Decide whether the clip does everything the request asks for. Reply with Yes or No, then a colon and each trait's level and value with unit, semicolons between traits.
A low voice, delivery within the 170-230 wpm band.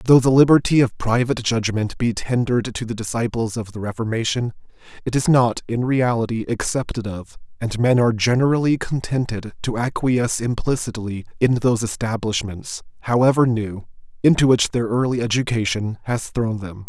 No: low, 115 Hz; average, 150 wpm